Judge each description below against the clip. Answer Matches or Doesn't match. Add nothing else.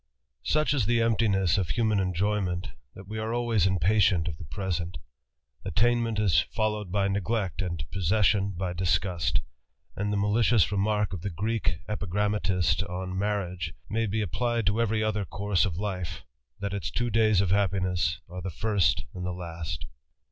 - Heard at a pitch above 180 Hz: Doesn't match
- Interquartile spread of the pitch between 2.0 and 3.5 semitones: Matches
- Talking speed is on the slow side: Doesn't match